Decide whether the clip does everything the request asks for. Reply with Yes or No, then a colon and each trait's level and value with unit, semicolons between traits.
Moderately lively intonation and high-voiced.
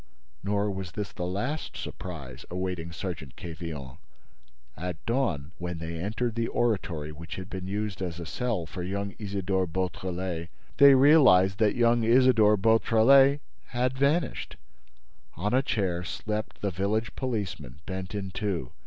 No: average, 4.6 semitones; very low, 95 Hz